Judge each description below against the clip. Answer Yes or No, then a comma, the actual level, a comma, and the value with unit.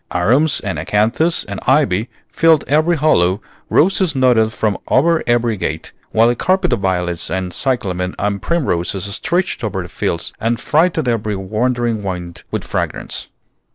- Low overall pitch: Yes, low, 115 Hz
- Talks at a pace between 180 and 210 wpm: No, average, 150 wpm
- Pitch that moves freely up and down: Yes, wide, 7.4 semitones